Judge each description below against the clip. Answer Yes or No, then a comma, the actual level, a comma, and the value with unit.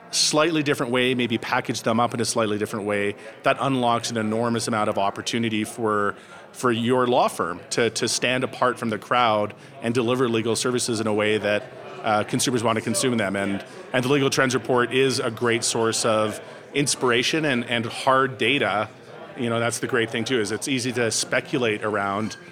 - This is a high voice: No, low, 120 Hz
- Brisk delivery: No, average, 195 wpm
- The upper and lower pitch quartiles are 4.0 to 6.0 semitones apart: No, average, 2.8 semitones